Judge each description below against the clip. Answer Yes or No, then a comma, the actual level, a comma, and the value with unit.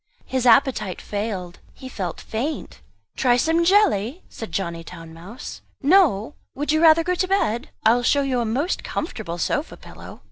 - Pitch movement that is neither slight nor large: No, wide, 7.5 semitones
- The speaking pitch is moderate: No, high, 245 Hz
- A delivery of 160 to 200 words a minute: Yes, average, 170 wpm